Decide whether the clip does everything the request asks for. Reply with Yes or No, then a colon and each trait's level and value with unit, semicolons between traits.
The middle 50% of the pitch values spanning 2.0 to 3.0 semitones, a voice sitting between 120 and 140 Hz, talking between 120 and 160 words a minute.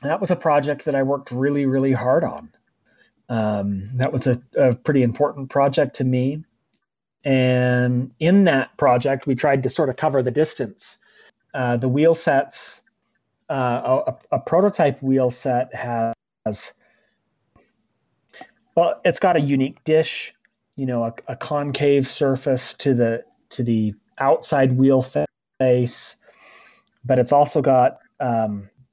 Yes: narrow, 2.6 semitones; low, 130 Hz; average, 140 wpm